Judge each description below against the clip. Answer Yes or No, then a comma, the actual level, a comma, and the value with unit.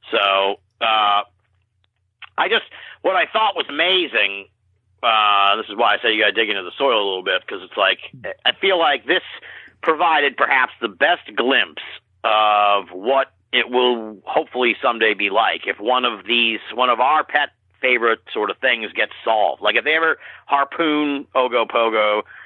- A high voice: No, low, 115 Hz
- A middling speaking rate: Yes, average, 175 wpm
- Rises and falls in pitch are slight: No, average, 5.0 semitones